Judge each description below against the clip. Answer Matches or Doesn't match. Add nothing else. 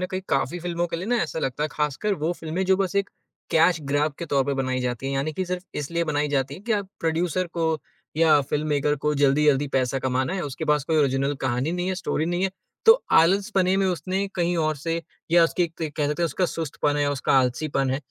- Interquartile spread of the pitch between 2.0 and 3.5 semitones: Doesn't match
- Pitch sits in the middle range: Matches